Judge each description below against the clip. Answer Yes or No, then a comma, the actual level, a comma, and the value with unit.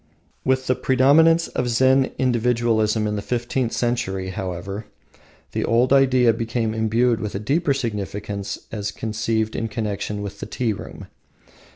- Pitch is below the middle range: Yes, low, 115 Hz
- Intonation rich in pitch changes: No, average, 3.4 semitones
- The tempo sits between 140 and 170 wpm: Yes, average, 145 wpm